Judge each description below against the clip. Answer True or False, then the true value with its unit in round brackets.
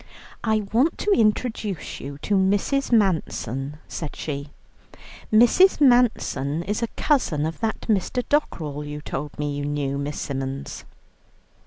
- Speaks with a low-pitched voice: False (175 Hz)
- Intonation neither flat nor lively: False (7.9 semitones)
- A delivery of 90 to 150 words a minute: True (135 wpm)